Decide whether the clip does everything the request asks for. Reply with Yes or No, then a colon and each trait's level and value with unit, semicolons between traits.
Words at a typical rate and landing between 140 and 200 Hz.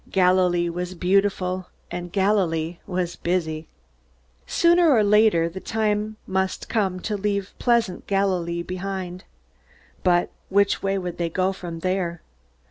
No: slow, 125 wpm; medium, 185 Hz